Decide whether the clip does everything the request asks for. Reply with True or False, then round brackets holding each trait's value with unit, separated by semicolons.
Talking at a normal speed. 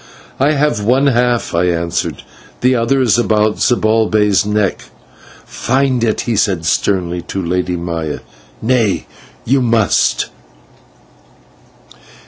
False (115 wpm)